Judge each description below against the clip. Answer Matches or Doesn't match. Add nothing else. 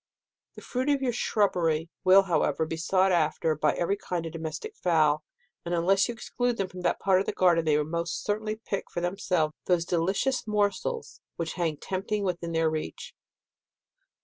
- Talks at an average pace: Matches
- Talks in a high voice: Doesn't match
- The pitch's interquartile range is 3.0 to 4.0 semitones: Matches